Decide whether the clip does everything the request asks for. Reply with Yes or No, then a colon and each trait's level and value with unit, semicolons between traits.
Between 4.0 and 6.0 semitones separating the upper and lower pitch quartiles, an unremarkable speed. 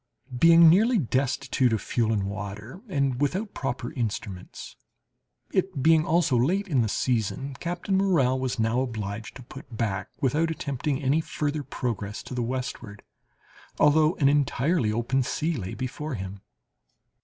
Yes: average, 5.3 semitones; average, 145 wpm